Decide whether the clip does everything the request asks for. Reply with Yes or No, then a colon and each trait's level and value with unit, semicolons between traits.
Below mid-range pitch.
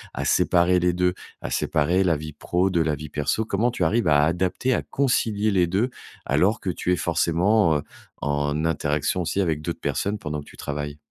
Yes: very low, 85 Hz